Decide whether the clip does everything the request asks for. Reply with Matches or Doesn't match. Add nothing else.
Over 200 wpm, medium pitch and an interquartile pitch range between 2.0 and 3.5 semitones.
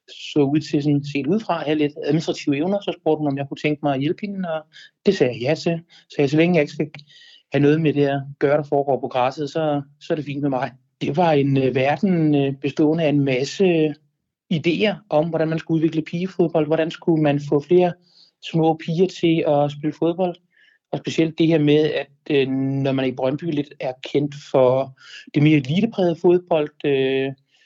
Matches